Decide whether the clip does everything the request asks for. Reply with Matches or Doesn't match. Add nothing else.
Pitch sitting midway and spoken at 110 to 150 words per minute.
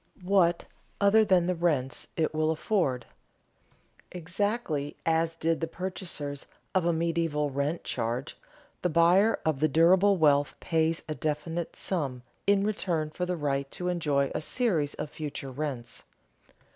Matches